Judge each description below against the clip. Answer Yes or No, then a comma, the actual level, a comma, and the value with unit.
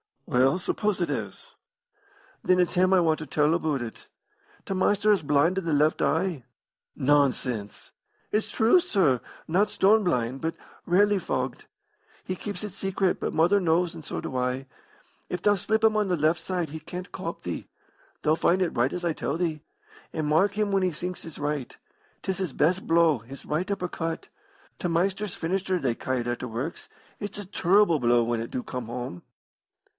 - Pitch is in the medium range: Yes, medium, 170 Hz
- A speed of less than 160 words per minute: No, average, 190 wpm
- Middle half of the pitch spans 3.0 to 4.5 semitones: No, average, 4.9 semitones